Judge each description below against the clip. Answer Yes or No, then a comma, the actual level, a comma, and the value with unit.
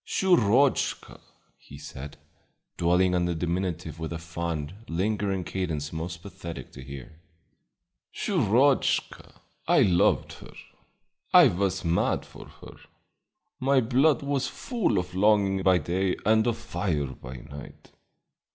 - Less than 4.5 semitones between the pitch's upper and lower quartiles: No, average, 4.9 semitones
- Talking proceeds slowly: Yes, slow, 125 wpm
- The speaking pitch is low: Yes, very low, 90 Hz